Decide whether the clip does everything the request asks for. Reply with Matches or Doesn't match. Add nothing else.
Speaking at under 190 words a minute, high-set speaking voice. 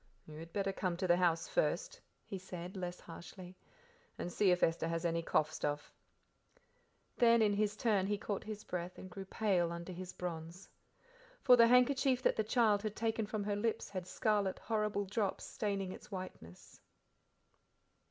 Matches